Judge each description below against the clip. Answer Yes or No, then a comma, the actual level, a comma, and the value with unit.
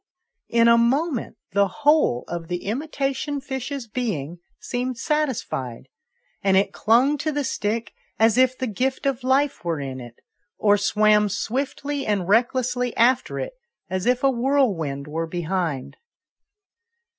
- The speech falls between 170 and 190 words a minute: No, average, 140 wpm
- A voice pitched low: No, high, 235 Hz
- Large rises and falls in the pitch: Yes, wide, 6.0 semitones